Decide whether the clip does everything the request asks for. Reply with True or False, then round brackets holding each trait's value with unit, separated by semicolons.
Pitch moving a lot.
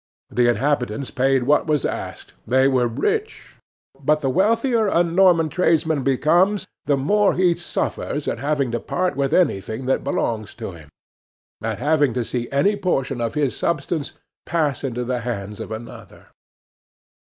True (5.7 semitones)